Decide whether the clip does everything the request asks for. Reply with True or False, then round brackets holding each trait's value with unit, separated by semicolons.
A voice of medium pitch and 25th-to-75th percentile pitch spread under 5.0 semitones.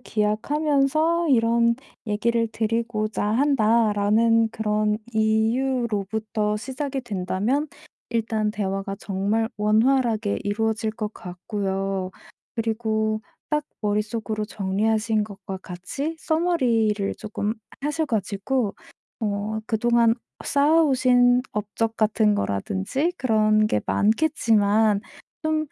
False (220 Hz; 2.5 semitones)